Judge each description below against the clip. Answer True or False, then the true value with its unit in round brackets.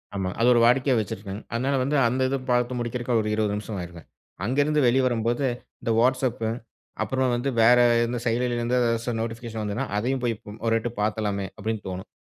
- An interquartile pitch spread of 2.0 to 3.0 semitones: True (2.5 semitones)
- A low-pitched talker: True (120 Hz)